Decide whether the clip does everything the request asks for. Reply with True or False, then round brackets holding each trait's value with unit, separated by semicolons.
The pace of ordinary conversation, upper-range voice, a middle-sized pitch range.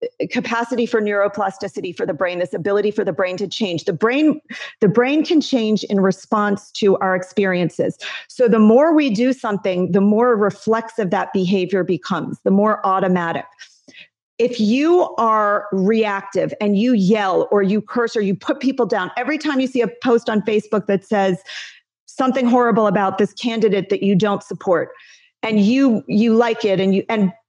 True (175 wpm; 215 Hz; 3.3 semitones)